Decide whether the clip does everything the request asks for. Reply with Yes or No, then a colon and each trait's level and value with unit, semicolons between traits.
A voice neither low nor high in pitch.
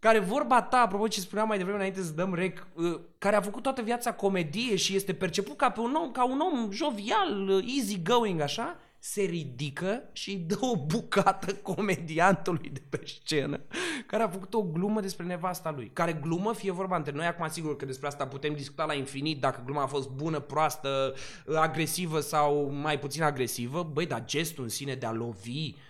Yes: medium, 175 Hz